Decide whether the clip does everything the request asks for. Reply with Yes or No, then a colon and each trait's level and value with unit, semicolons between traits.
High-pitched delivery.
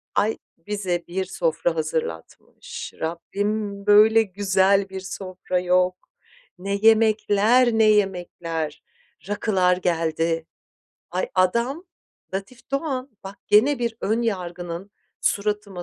Yes: high, 195 Hz